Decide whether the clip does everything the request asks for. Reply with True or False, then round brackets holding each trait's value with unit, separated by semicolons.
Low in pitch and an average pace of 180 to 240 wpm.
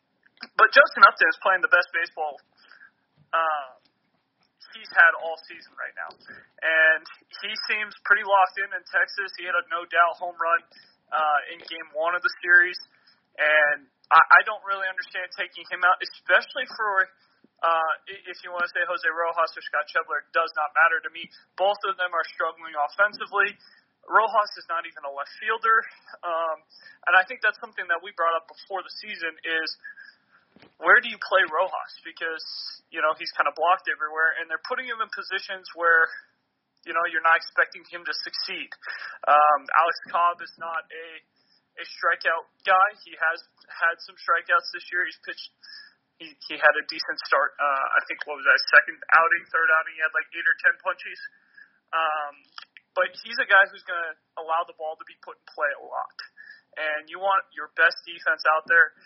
False (175 Hz; 185 wpm)